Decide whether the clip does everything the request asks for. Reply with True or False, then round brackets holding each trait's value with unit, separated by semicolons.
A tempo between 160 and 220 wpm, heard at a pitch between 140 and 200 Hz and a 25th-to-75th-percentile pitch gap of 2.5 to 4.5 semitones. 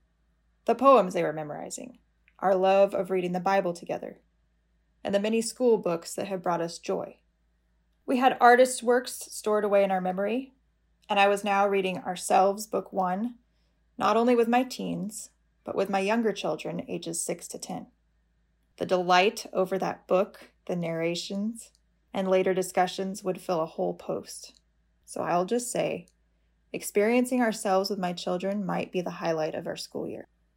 True (165 wpm; 190 Hz; 3.8 semitones)